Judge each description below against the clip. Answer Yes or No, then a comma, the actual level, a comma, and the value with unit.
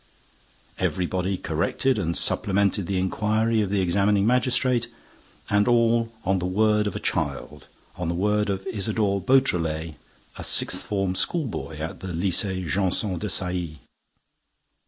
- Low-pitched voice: Yes, low, 100 Hz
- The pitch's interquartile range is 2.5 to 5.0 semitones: Yes, average, 3.1 semitones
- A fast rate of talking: No, slow, 135 wpm